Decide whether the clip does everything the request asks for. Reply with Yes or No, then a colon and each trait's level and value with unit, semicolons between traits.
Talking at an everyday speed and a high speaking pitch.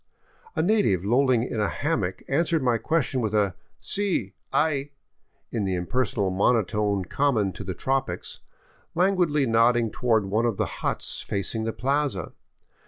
No: average, 160 wpm; low, 115 Hz